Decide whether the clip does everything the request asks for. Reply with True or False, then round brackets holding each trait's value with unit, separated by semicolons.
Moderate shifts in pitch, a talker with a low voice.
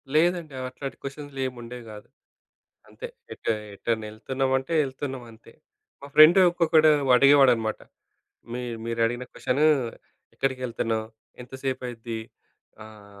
True (3.2 semitones; 130 Hz)